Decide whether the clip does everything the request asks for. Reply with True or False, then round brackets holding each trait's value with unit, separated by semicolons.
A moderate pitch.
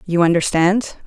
True (180 Hz)